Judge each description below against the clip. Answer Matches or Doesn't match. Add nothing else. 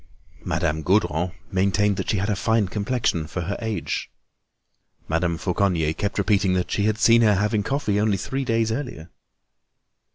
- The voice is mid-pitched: Doesn't match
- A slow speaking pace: Doesn't match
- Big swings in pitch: Doesn't match